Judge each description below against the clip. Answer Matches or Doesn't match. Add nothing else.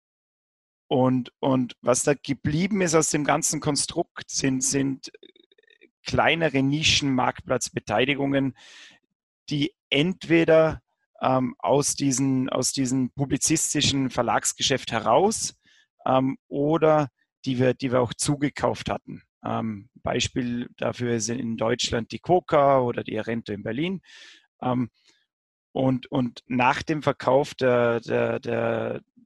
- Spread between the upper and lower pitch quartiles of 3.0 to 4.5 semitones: Matches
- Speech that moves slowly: Matches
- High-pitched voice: Doesn't match